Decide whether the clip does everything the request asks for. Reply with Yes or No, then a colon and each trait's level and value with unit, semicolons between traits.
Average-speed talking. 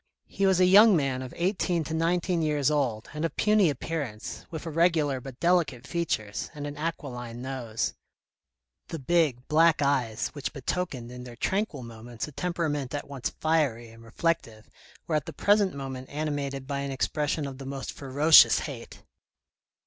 Yes: average, 165 wpm